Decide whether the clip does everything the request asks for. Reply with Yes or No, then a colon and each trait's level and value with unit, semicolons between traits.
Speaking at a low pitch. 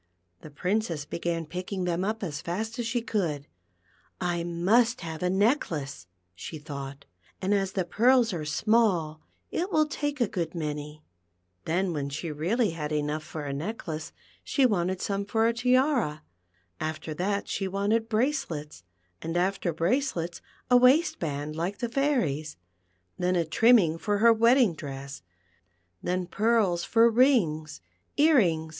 No: medium, 180 Hz